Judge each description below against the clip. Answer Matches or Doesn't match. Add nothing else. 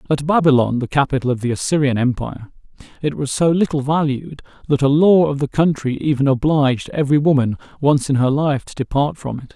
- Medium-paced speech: Matches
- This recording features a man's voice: Matches